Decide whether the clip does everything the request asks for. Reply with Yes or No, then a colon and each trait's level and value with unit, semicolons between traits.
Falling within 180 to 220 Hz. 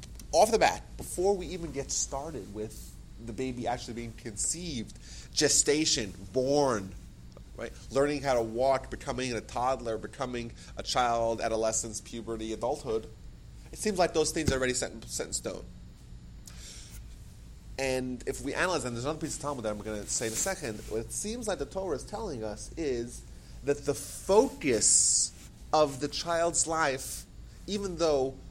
No: low, 125 Hz